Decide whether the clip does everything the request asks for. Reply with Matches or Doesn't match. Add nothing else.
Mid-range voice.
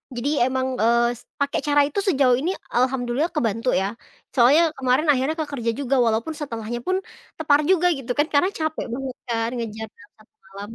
Doesn't match